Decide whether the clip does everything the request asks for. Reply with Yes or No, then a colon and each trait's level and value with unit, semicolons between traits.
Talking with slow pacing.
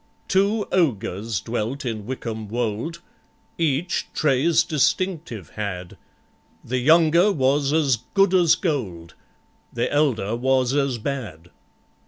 Yes: slow, 110 wpm